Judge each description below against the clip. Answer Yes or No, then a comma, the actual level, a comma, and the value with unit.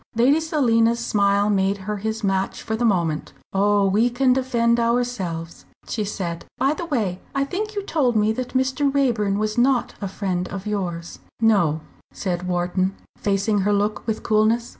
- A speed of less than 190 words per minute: Yes, average, 170 wpm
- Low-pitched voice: No, high, 215 Hz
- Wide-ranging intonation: No, average, 4.0 semitones